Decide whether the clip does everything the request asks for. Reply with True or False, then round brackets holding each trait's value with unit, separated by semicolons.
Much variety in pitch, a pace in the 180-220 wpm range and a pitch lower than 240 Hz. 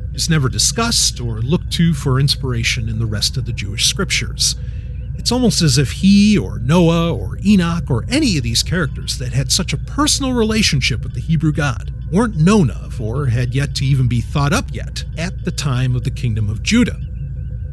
True (5.8 semitones; 200 wpm; 135 Hz)